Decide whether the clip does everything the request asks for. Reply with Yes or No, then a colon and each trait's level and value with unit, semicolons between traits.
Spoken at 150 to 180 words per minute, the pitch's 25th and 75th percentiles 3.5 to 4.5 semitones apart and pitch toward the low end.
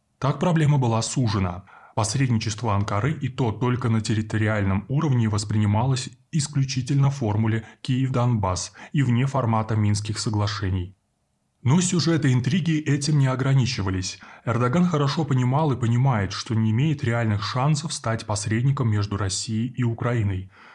No: average, 125 wpm; average, 4.2 semitones; low, 120 Hz